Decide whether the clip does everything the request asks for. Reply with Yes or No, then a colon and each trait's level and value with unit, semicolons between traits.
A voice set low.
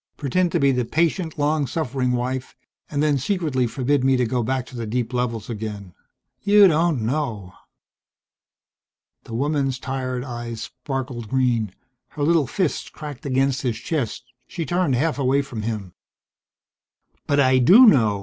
Yes: low, 130 Hz